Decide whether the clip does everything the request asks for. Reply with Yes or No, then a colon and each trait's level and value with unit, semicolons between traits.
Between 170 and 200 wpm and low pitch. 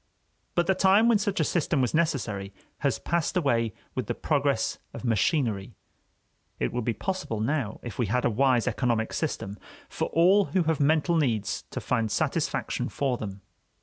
Yes: average, 175 wpm; low, 130 Hz